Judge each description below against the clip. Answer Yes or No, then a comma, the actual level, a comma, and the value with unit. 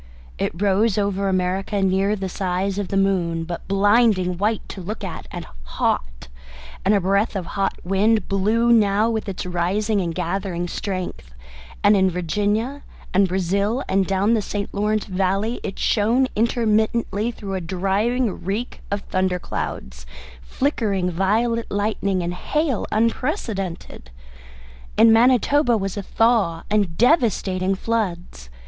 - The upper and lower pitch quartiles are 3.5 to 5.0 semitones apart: No, average, 3.0 semitones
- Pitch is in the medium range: No, high, 200 Hz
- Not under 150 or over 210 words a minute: No, average, 140 wpm